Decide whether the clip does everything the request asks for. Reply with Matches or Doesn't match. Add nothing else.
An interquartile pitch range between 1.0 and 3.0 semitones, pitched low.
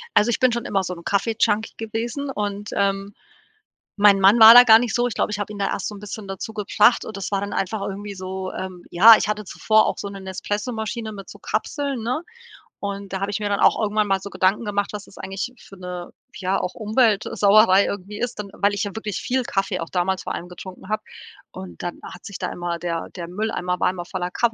Doesn't match